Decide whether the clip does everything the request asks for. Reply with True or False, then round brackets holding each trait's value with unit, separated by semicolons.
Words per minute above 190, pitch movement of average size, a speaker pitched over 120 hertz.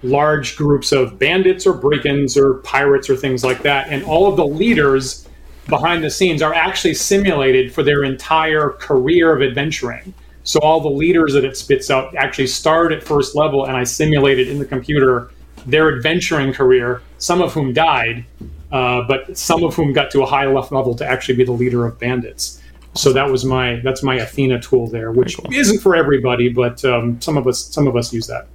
True (200 wpm; 3.4 semitones; 135 Hz)